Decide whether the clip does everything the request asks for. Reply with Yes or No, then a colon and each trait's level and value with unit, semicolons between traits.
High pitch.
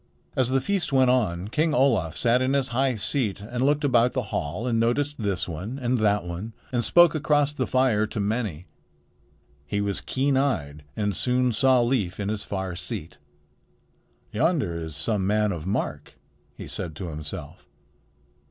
No: low, 115 Hz